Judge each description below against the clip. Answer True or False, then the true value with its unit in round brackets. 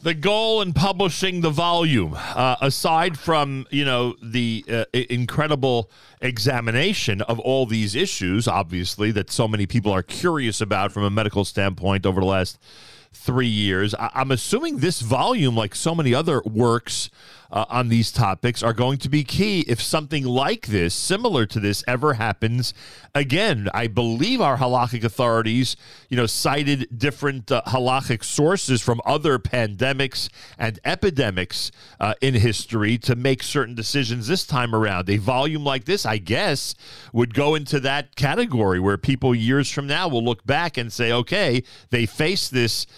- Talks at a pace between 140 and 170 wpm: True (160 wpm)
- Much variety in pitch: False (4.2 semitones)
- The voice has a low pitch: True (125 Hz)